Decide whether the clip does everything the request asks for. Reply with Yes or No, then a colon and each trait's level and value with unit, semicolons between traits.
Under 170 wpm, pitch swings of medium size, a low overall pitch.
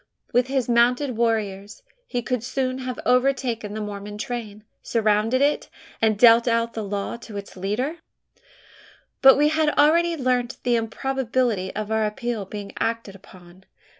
No: average, 150 wpm; average, 3.5 semitones; high, 235 Hz